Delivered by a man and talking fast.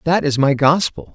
Yes: male; fast, 210 wpm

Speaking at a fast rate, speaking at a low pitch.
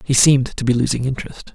Yes: fast, 235 wpm; low, 130 Hz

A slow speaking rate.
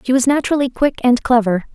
No: fast, 205 wpm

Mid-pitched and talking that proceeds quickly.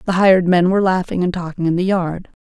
Yes: medium, 180 Hz; fast, 245 wpm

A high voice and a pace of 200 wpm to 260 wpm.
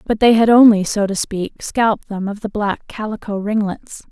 Yes: high, 210 Hz; fast, 205 wpm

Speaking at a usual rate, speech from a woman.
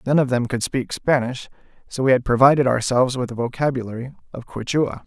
No: average, 190 wpm; male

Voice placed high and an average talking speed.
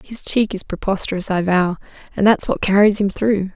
Yes: high, 195 Hz; average, 185 wpm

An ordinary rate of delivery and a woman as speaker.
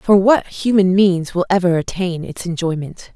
Yes: average, 170 wpm; female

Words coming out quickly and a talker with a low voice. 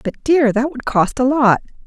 No: fast, 225 wpm; very high, 260 Hz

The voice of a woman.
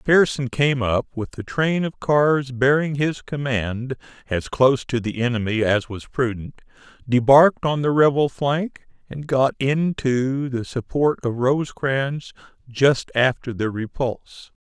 No: male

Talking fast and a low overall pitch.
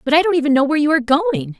No: fast, 340 wpm; very high, 295 Hz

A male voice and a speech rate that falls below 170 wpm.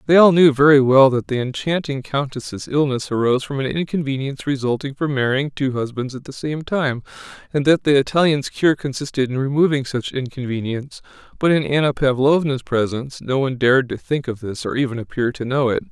No: male; average, 190 wpm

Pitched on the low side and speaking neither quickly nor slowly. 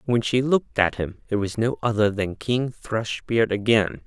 Yes: low, 110 Hz; average, 190 wpm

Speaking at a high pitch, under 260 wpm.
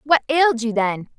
Yes: very high, 255 Hz; average, 200 wpm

